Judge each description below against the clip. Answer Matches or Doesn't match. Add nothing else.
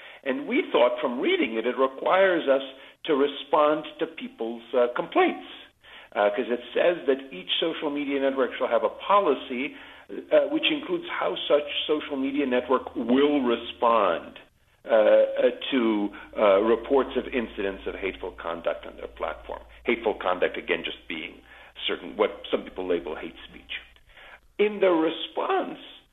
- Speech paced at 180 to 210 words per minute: Doesn't match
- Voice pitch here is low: Doesn't match